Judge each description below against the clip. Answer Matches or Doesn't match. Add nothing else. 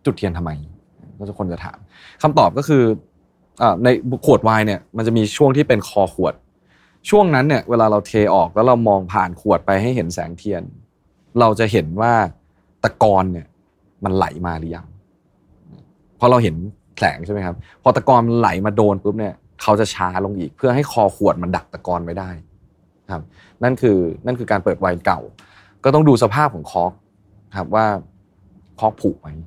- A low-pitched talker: Matches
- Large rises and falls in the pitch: Doesn't match